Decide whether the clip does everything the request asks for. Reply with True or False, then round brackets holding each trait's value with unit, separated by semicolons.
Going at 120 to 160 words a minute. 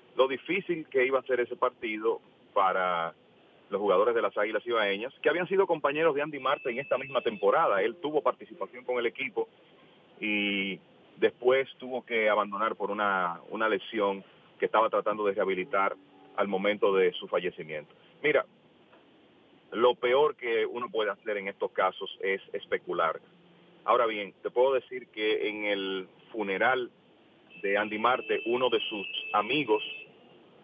True (155 wpm)